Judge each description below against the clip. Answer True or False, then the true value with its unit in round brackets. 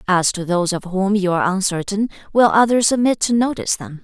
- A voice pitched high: True (200 Hz)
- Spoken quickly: True (210 wpm)